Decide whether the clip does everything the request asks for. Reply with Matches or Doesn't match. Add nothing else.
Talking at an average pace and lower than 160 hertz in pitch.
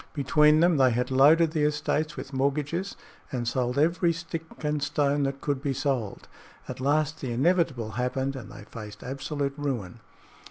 Matches